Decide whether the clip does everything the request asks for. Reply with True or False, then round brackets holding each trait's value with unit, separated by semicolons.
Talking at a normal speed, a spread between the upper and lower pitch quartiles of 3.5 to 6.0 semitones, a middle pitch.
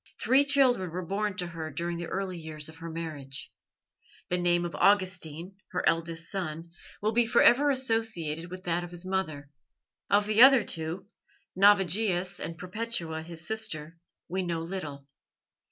True (160 wpm; 3.8 semitones; 175 Hz)